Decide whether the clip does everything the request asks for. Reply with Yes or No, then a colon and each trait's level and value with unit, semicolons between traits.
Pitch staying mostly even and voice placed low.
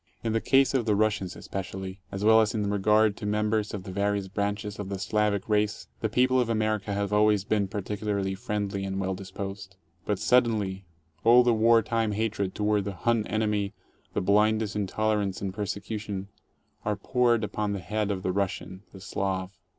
Yes: narrow, 1.8 semitones; low, 105 Hz